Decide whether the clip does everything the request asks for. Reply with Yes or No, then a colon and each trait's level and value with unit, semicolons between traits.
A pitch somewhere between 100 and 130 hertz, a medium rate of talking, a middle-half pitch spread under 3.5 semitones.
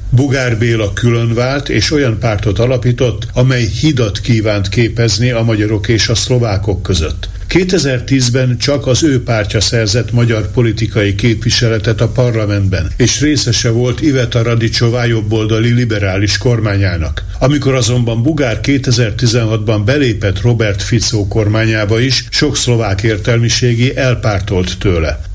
Yes: low, 115 Hz; average, 120 wpm; narrow, 2.6 semitones